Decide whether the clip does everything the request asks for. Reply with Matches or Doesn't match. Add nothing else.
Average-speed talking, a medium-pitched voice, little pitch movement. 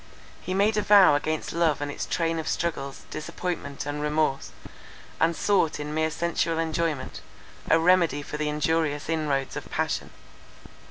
Matches